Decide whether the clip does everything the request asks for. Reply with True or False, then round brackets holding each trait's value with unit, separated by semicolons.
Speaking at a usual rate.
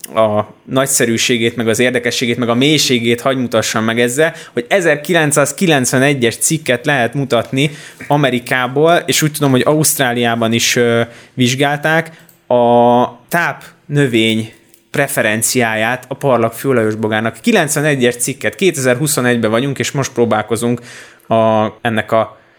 True (115 wpm)